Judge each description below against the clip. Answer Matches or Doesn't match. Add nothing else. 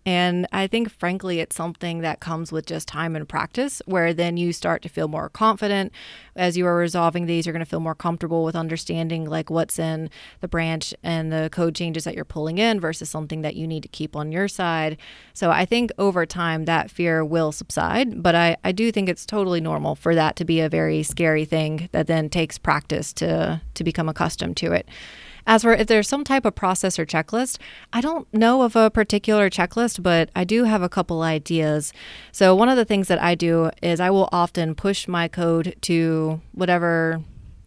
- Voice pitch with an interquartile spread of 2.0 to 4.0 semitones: Matches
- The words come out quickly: Matches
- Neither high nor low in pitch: Matches